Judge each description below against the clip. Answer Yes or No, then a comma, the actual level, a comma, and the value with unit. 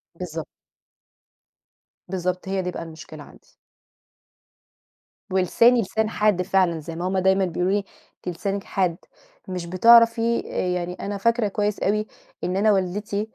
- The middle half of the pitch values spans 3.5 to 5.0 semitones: No, average, 2.7 semitones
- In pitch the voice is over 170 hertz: Yes, high, 190 Hz